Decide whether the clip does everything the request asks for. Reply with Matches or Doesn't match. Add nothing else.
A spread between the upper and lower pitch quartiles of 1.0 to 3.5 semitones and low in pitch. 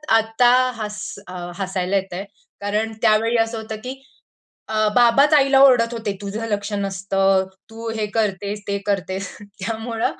Doesn't match